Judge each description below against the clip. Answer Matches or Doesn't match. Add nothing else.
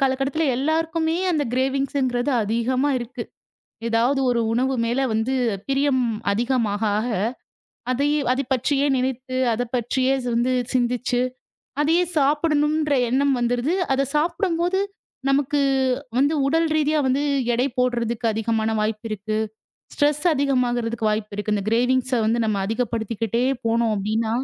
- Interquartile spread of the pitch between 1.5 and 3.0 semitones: Doesn't match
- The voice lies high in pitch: Matches